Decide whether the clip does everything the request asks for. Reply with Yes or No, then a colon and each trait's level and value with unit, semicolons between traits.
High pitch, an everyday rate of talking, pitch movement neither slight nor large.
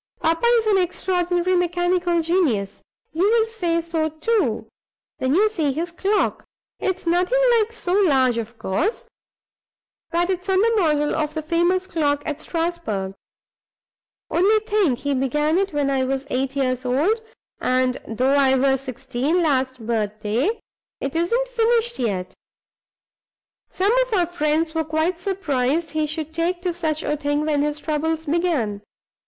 Yes: very high, 320 Hz; average, 150 wpm; average, 5.0 semitones